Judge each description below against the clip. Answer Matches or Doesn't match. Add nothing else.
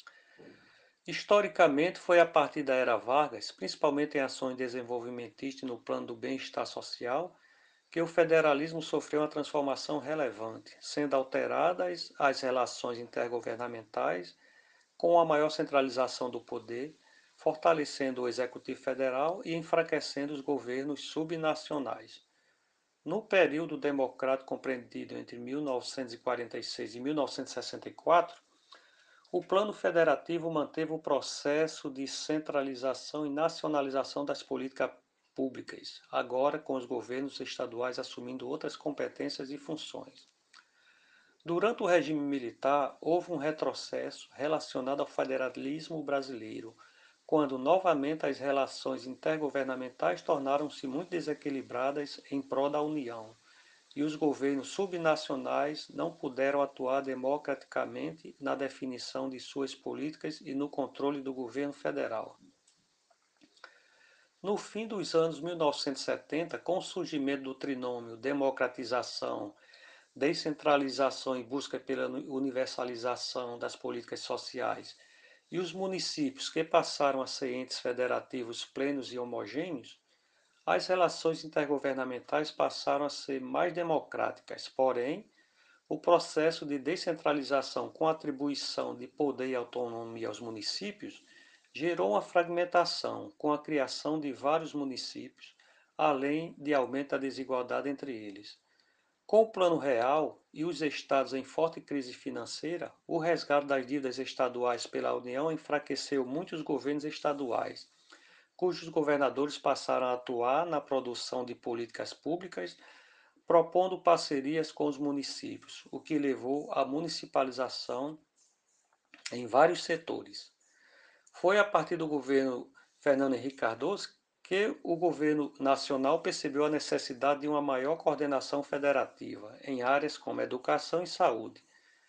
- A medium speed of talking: Doesn't match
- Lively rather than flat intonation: Doesn't match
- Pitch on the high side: Doesn't match